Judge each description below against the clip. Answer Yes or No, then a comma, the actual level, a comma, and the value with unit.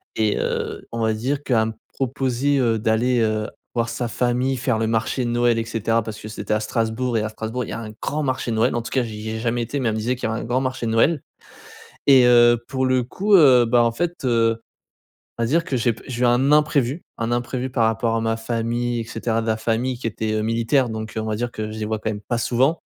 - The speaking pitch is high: No, low, 120 Hz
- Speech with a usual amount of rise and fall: No, narrow, 2.3 semitones